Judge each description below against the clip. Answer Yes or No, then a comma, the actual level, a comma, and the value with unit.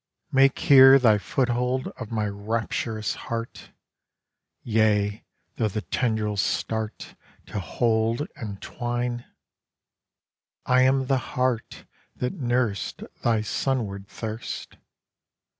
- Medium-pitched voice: No, low, 115 Hz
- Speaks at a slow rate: Yes, slow, 100 wpm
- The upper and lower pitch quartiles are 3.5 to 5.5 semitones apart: No, average, 2.8 semitones